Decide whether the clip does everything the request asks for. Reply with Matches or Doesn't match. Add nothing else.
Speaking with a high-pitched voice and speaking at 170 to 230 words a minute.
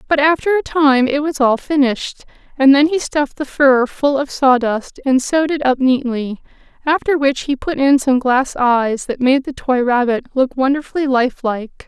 Matches